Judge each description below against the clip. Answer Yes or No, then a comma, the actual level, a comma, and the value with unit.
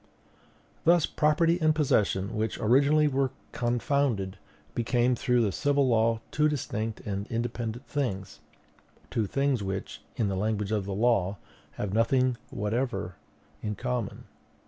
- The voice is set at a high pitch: No, low, 115 Hz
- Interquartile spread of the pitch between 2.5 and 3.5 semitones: No, average, 4.7 semitones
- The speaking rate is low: Yes, slow, 130 wpm